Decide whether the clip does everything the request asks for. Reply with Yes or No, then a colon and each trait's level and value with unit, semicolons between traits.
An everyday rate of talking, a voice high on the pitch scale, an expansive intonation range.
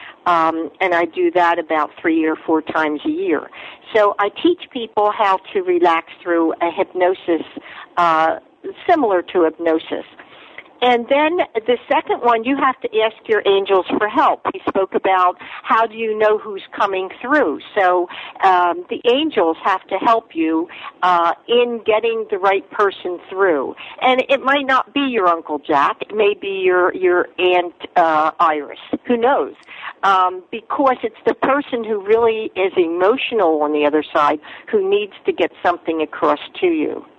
Yes: average, 165 wpm; high, 205 Hz; wide, 7.2 semitones